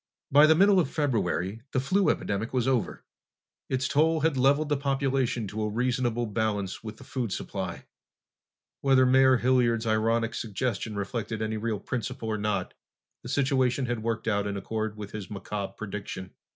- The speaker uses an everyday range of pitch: Yes, average, 3.8 semitones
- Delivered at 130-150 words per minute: No, average, 165 wpm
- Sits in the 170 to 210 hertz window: No, low, 115 Hz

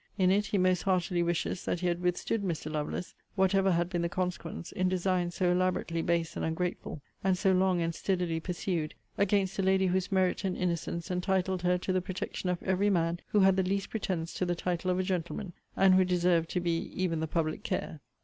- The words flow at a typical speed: No, fast, 215 wpm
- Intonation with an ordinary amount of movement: No, narrow, 1.6 semitones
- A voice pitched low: No, medium, 180 Hz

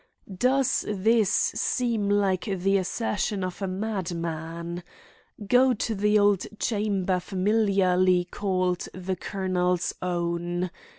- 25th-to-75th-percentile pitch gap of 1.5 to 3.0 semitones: Yes, narrow, 2.6 semitones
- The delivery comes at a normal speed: No, slow, 105 wpm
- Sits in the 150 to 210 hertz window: Yes, high, 190 Hz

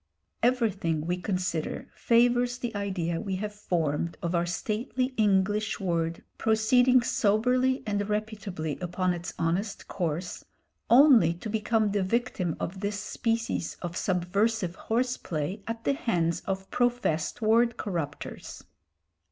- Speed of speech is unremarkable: No, slow, 125 wpm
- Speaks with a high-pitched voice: Yes, high, 205 Hz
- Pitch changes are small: No, average, 4.7 semitones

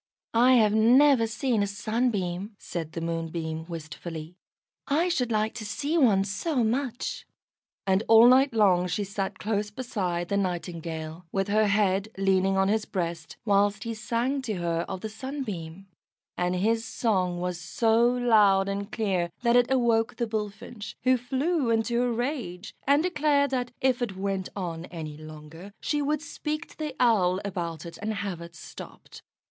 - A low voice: No, high, 210 Hz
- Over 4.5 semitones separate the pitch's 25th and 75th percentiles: Yes, average, 5.2 semitones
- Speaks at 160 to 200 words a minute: Yes, average, 165 wpm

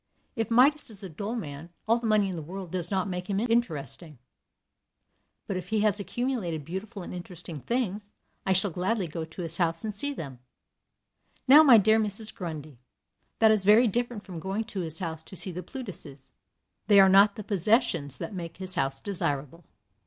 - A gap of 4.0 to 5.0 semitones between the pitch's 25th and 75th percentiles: Yes, average, 4.6 semitones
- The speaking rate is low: No, average, 190 wpm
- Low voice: No, high, 190 Hz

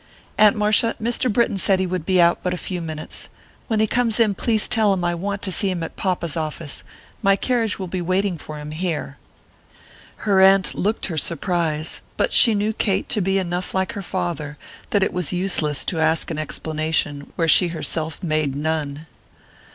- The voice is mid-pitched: Yes, medium, 180 Hz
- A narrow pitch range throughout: No, average, 3.9 semitones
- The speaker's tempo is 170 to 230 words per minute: Yes, average, 195 wpm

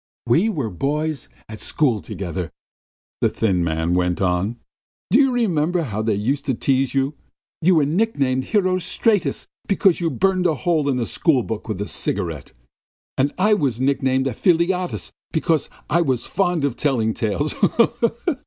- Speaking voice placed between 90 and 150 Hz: Yes, medium, 140 Hz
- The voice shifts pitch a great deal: Yes, wide, 7.6 semitones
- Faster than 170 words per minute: No, average, 155 wpm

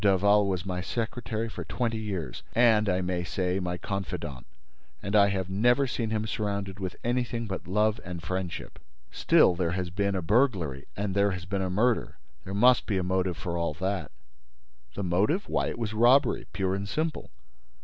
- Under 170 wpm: No, average, 185 wpm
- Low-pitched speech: Yes, low, 100 Hz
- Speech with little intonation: No, average, 3.2 semitones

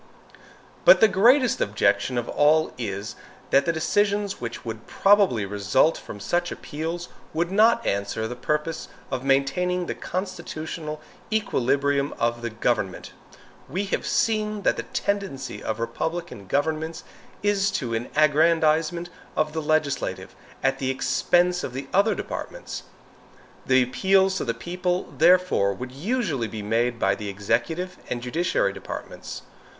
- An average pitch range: No, wide, 7.0 semitones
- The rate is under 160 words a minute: Yes, average, 140 wpm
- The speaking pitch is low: No, medium, 155 Hz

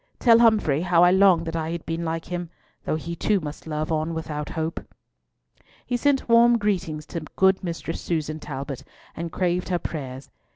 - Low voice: No, medium, 170 Hz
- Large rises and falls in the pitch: No, average, 3.3 semitones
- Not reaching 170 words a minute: No, average, 180 wpm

